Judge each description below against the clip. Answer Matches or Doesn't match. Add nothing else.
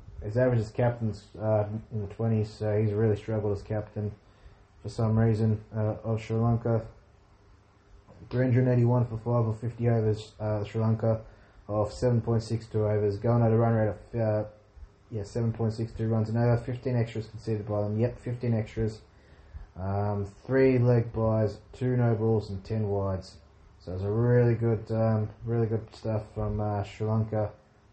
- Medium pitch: Doesn't match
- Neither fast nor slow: Matches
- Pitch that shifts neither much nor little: Doesn't match